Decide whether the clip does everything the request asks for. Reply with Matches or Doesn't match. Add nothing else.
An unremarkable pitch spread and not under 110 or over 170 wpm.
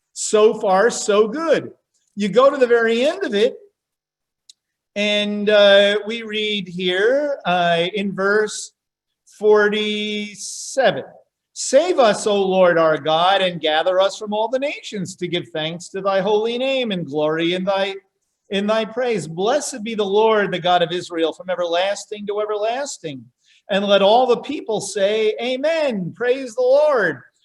Matches